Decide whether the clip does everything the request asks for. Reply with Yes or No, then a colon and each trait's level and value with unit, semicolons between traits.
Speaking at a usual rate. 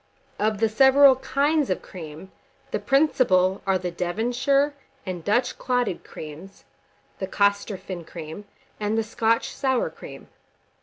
No: slow, 125 wpm